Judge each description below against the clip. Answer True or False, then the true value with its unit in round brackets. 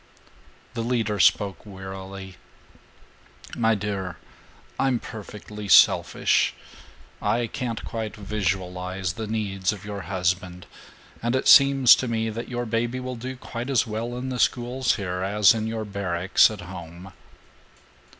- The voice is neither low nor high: False (105 Hz)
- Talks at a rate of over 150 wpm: False (135 wpm)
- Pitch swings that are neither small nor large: True (3.8 semitones)